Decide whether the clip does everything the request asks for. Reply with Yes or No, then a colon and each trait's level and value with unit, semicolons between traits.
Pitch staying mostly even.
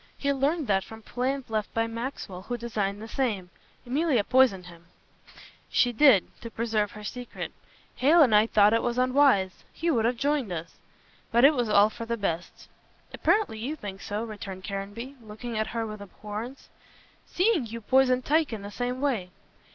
No: average, 4.0 semitones